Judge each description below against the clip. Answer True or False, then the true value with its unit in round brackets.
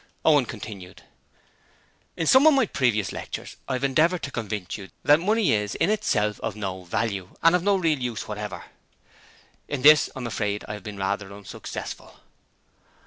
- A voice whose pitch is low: True (115 Hz)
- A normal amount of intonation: False (7.5 semitones)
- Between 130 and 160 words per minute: False (175 wpm)